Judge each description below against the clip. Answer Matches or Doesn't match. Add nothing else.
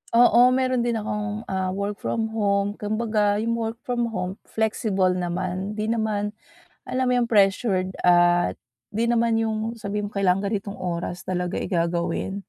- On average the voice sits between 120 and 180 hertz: Doesn't match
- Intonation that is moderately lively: Matches